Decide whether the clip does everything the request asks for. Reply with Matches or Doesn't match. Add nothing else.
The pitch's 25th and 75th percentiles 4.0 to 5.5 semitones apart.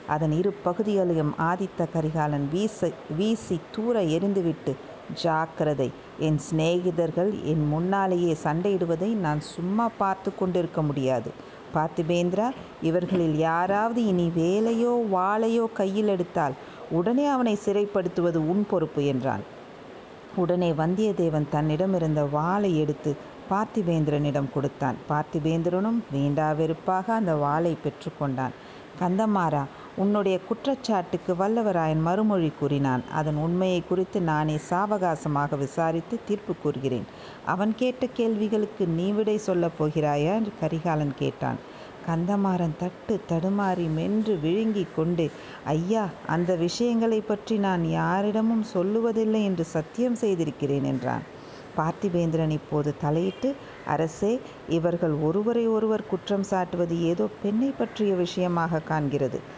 Matches